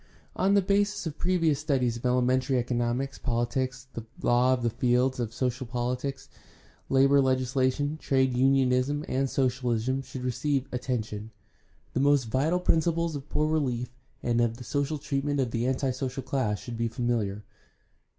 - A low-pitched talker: Yes, low, 130 Hz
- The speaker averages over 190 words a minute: No, average, 150 wpm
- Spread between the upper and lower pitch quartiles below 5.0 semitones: Yes, narrow, 2.5 semitones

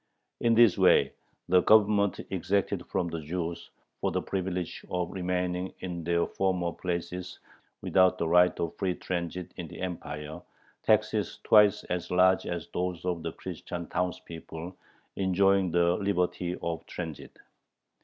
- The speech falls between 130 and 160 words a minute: Yes, average, 140 wpm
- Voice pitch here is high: No, very low, 90 Hz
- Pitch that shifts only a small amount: Yes, narrow, 1.6 semitones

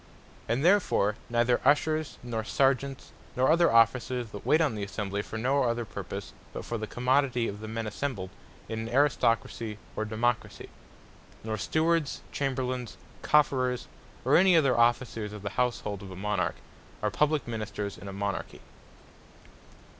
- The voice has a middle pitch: No, low, 120 Hz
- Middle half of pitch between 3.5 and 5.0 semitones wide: Yes, average, 4.1 semitones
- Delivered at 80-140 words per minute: No, average, 155 wpm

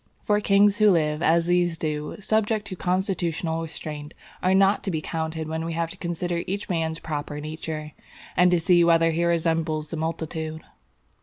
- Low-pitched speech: No, medium, 165 Hz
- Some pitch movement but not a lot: No, narrow, 2.1 semitones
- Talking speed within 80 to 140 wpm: No, average, 175 wpm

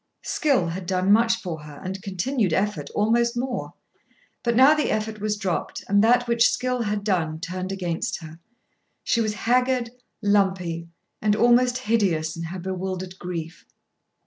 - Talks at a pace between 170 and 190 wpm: No, average, 155 wpm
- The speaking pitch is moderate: No, high, 205 Hz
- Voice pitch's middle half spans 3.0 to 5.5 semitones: Yes, average, 4.6 semitones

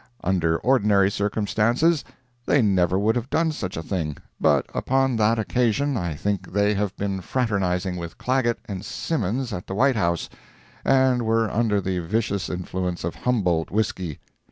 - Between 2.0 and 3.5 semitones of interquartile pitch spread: No, average, 4.8 semitones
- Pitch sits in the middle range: No, low, 105 Hz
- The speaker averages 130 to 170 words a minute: Yes, average, 155 wpm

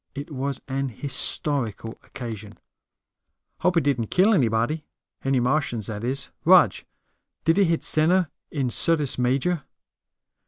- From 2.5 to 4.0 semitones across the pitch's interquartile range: No, average, 4.6 semitones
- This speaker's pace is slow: Yes, slow, 130 wpm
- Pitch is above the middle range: No, low, 135 Hz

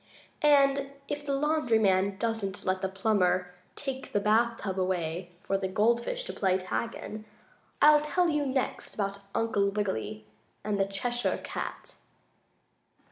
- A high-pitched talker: Yes, high, 215 Hz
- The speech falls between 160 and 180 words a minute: No, average, 150 wpm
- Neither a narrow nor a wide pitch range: No, wide, 5.8 semitones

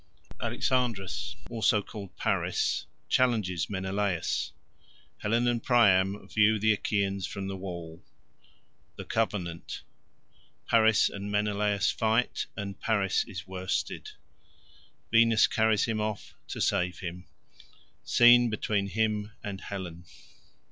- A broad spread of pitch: No, average, 2.9 semitones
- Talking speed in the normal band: No, slow, 95 wpm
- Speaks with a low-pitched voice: Yes, low, 100 Hz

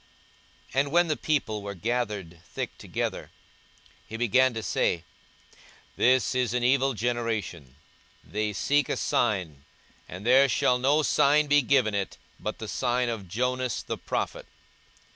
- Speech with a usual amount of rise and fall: Yes, average, 3.9 semitones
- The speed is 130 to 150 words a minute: Yes, average, 145 wpm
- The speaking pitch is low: Yes, low, 120 Hz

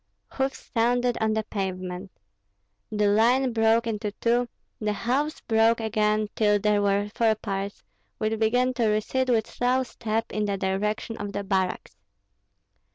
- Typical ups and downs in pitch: No, narrow, 2.3 semitones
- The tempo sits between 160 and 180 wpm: No, average, 150 wpm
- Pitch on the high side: Yes, high, 220 Hz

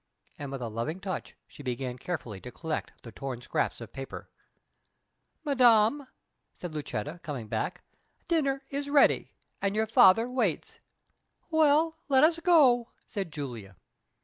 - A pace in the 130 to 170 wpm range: Yes, average, 140 wpm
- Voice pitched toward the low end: No, high, 190 Hz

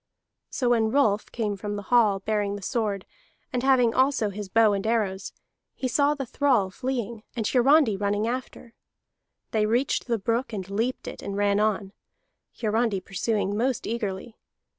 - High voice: Yes, high, 220 Hz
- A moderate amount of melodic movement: Yes, average, 3.2 semitones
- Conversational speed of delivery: Yes, average, 160 wpm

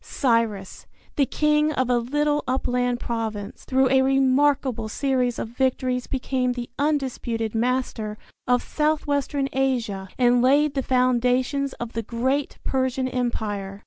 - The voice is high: Yes, very high, 255 Hz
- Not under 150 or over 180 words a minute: No, slow, 135 wpm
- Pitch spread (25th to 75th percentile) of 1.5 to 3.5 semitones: Yes, narrow, 2.4 semitones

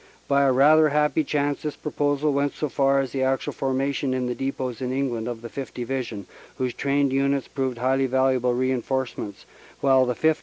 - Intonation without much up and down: Yes, narrow, 1.7 semitones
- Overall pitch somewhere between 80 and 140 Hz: Yes, low, 135 Hz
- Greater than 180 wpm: Yes, average, 190 wpm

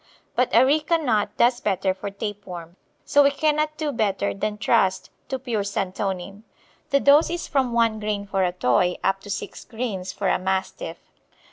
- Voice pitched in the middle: No, high, 210 Hz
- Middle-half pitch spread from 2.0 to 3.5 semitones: No, wide, 5.5 semitones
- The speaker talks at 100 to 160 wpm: No, average, 175 wpm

